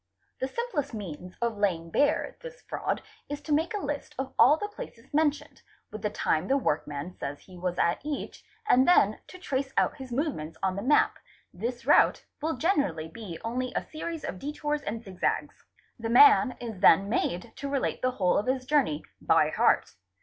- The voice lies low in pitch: No, very high, 255 Hz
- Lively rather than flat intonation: Yes, wide, 7.8 semitones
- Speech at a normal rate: Yes, average, 195 wpm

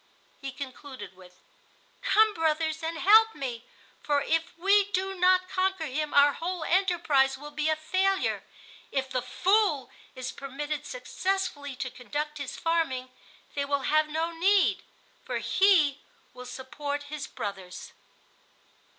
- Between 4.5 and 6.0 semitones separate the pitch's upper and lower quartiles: Yes, average, 5.3 semitones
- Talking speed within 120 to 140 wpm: Yes, slow, 135 wpm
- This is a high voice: Yes, very high, 305 Hz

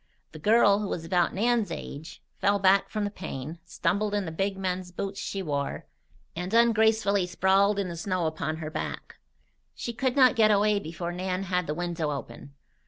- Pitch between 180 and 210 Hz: Yes, high, 190 Hz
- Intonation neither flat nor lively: Yes, average, 3.2 semitones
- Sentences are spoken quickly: No, average, 190 wpm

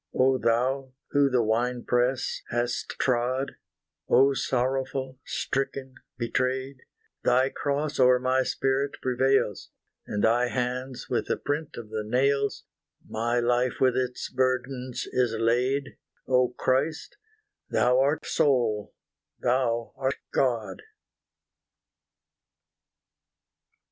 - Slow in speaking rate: Yes, slow, 105 wpm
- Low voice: Yes, low, 130 Hz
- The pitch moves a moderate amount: No, narrow, 1.6 semitones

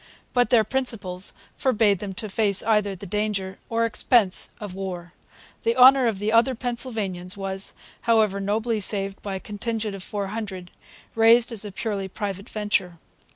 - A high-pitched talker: Yes, high, 210 Hz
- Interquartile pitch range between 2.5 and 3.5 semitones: Yes, average, 2.8 semitones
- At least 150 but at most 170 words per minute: Yes, average, 160 wpm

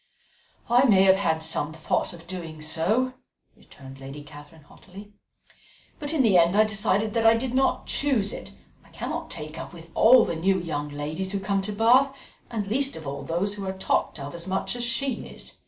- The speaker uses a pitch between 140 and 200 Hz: Yes, high, 190 Hz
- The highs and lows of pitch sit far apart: Yes, wide, 5.9 semitones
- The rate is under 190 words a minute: No, fast, 205 wpm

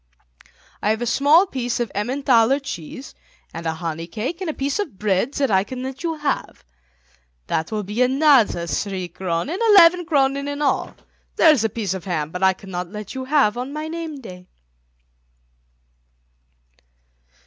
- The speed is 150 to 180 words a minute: Yes, average, 170 wpm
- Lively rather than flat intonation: Yes, wide, 7.0 semitones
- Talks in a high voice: Yes, high, 245 Hz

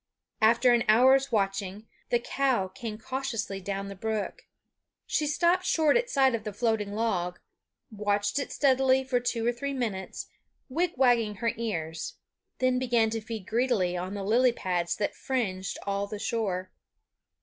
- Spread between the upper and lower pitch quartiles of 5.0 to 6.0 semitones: No, average, 4.4 semitones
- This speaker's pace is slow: No, average, 155 wpm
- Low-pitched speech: No, high, 225 Hz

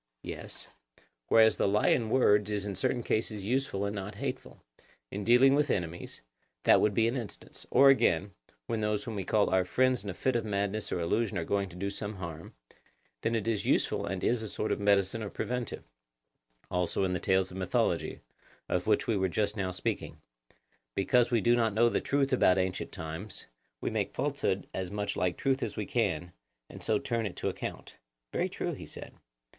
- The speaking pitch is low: Yes, low, 105 Hz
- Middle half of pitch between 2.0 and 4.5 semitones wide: Yes, average, 3.5 semitones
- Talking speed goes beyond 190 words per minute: Yes, average, 200 wpm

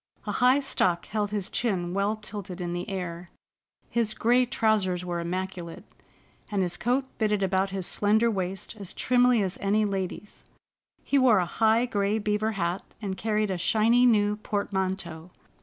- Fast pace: No, average, 160 wpm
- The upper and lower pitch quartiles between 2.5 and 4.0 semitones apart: Yes, average, 2.9 semitones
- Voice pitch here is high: Yes, high, 205 Hz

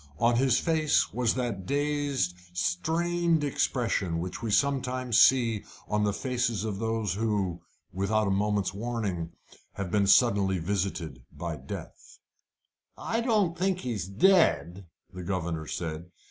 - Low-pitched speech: Yes, low, 105 Hz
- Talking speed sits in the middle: No, slow, 130 wpm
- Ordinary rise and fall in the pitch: No, wide, 5.9 semitones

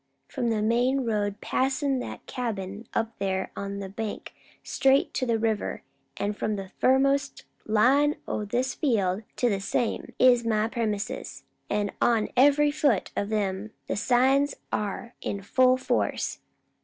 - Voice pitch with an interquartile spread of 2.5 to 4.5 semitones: Yes, average, 4.0 semitones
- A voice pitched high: Yes, high, 230 Hz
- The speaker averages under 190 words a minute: Yes, average, 150 wpm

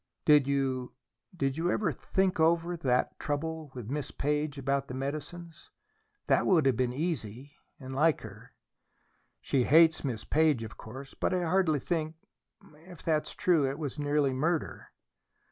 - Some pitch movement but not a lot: Yes, average, 3.4 semitones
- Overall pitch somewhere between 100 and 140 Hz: No, medium, 150 Hz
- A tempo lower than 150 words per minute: No, average, 155 wpm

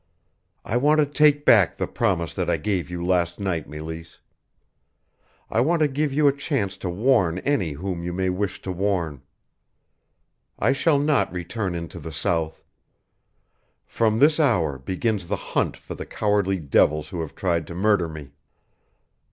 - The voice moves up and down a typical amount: No, wide, 6.3 semitones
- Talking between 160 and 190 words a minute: Yes, average, 165 wpm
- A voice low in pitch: Yes, very low, 95 Hz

